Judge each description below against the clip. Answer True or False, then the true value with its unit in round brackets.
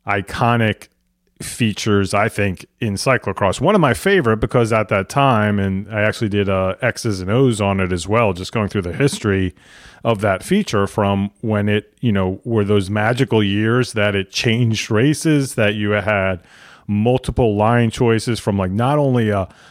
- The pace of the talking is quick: False (175 wpm)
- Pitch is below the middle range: True (105 Hz)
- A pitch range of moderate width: True (3.1 semitones)